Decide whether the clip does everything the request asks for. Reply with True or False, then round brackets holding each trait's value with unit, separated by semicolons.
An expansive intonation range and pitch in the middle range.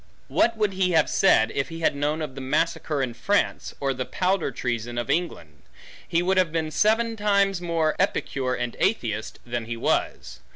True (7.4 semitones; 155 Hz)